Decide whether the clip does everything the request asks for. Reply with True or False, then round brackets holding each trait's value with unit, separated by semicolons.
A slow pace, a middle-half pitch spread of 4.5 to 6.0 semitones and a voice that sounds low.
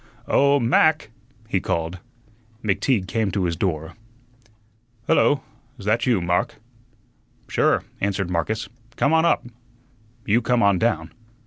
True (120 wpm; 5.3 semitones; 105 Hz)